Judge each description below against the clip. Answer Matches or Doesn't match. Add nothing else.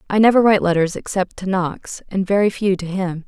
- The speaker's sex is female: Matches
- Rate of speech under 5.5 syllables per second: Doesn't match